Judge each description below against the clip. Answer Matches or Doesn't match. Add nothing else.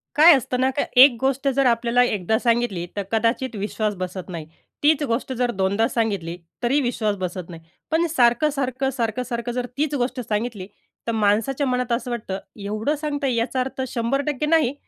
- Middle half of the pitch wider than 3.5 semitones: Matches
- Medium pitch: Doesn't match